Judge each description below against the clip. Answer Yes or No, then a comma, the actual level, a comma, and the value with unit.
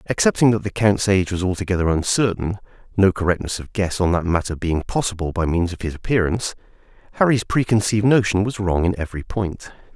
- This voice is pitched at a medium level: No, very low, 95 Hz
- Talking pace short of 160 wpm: No, average, 180 wpm